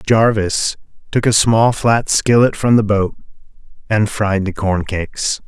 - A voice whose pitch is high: No, low, 105 Hz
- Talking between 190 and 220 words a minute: No, average, 155 wpm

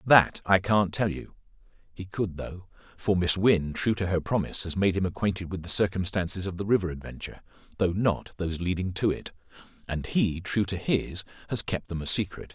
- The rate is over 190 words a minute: Yes, average, 200 wpm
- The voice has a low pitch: Yes, very low, 95 Hz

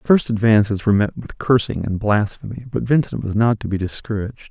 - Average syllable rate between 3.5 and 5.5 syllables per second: No, 6.1 syllables/s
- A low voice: Yes, low, 110 Hz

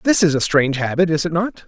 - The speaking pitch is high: No, medium, 165 Hz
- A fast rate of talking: Yes, fast, 285 wpm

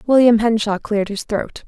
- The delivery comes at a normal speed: Yes, average, 180 wpm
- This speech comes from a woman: Yes, female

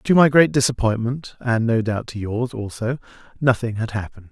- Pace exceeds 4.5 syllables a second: No, 4.2 syllables/s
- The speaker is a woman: No, male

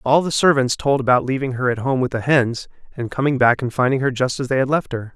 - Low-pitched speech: Yes, low, 130 Hz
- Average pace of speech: No, fast, 280 wpm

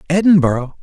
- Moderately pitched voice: Yes, medium, 160 Hz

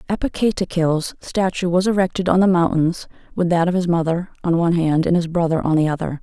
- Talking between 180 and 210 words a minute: Yes, average, 200 wpm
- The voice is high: No, medium, 175 Hz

